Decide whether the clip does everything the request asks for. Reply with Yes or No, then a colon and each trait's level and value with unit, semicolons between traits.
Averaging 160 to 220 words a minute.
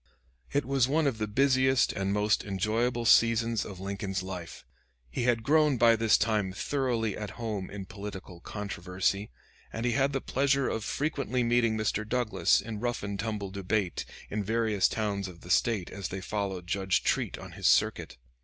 Yes: average, 175 wpm